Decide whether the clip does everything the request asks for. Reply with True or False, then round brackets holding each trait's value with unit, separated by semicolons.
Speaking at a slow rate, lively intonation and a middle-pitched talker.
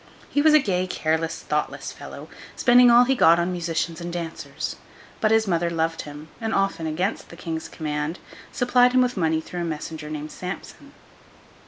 False (180 wpm; 5.7 semitones; 170 Hz)